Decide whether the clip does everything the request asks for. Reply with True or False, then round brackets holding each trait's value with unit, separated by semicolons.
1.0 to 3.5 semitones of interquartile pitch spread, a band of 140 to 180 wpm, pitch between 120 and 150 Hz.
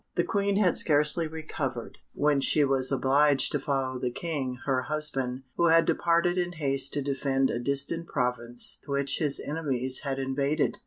True (2.9 semitones; 165 wpm; 140 Hz)